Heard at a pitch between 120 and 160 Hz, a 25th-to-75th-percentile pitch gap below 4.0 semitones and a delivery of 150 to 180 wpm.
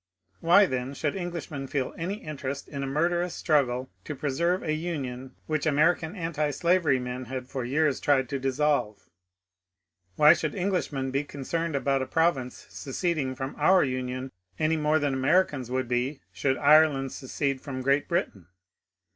Yes: medium, 140 Hz; average, 3.3 semitones; average, 160 wpm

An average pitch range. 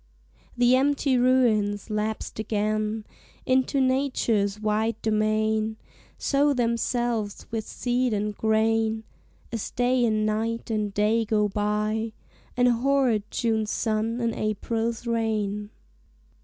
No: narrow, 2.2 semitones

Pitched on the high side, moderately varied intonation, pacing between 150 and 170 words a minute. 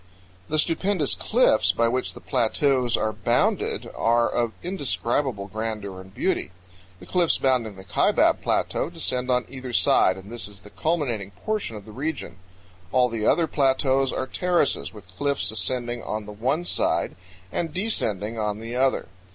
No: low, 120 Hz; average, 4.8 semitones; average, 160 wpm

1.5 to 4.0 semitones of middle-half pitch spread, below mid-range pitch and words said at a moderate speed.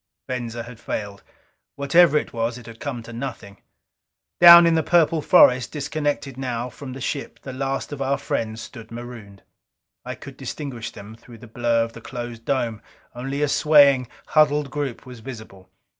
Yes: average, 3.5 semitones; low, 125 Hz; average, 175 wpm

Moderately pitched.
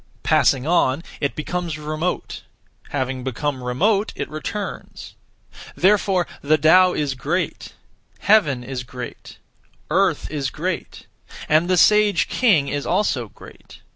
Yes: medium, 155 Hz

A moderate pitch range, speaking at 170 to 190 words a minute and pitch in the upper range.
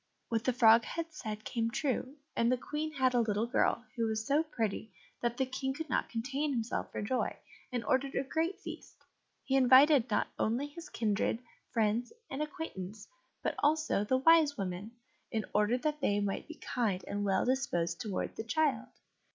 Yes: average, 4.5 semitones; average, 185 wpm; high, 245 Hz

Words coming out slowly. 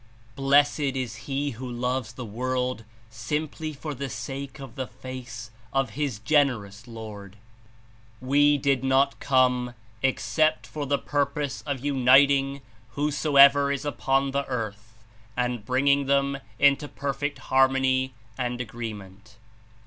Yes: slow, 130 wpm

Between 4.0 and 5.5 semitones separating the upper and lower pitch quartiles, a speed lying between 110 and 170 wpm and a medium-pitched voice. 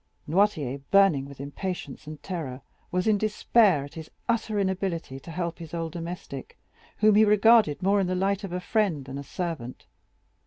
No: average, 5.2 semitones; average, 180 wpm; medium, 180 Hz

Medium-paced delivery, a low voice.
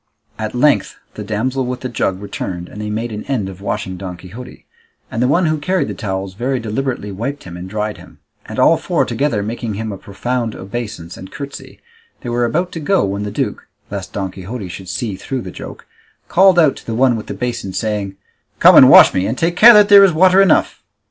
No: fast, 225 wpm; low, 110 Hz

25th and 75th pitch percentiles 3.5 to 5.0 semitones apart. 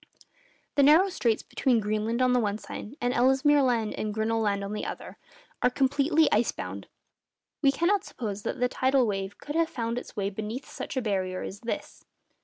Yes: average, 4.4 semitones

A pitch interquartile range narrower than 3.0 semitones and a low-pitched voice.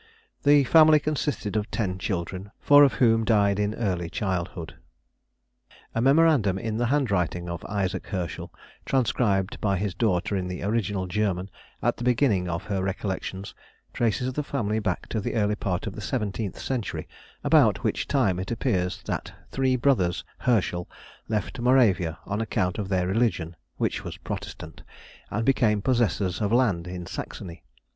No: average, 4.5 semitones; low, 105 Hz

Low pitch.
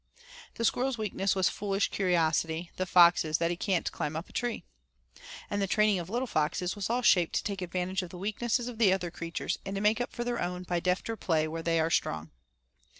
No: medium, 185 Hz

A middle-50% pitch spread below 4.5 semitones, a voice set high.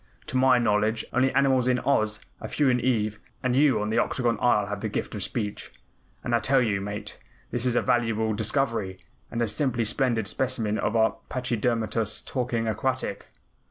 No: average, 3.1 semitones; low, 115 Hz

